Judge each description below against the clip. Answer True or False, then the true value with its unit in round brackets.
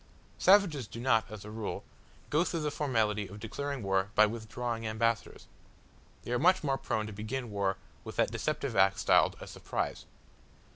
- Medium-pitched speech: False (115 Hz)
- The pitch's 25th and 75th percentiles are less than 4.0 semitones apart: False (4.3 semitones)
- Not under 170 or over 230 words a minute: True (175 wpm)